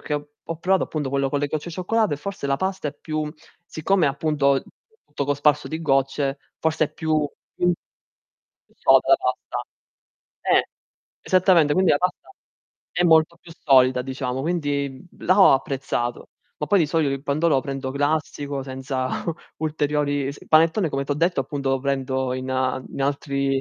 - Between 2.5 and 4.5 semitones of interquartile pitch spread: Yes, average, 2.8 semitones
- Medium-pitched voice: Yes, medium, 145 Hz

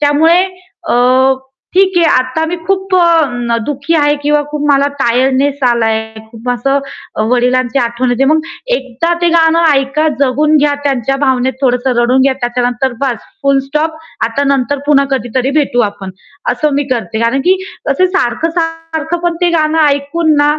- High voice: Yes, very high, 275 Hz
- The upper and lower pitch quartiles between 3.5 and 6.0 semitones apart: Yes, average, 4.1 semitones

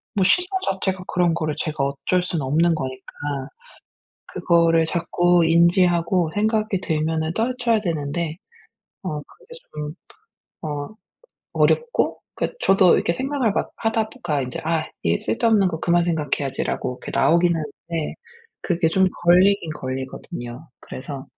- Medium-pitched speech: Yes, medium, 170 Hz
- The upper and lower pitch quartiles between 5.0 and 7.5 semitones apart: No, average, 3.7 semitones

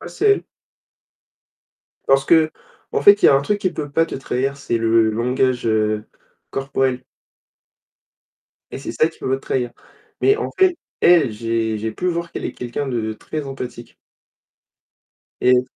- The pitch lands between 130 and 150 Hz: Yes, low, 135 Hz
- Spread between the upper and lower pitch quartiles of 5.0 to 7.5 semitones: Yes, average, 5.3 semitones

